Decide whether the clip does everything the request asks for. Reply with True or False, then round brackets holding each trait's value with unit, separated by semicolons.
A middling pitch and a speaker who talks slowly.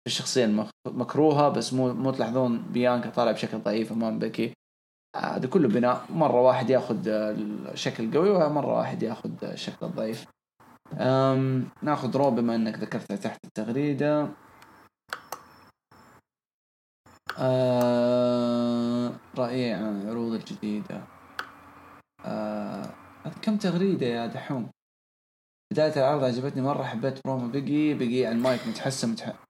False (125 Hz; 110 wpm)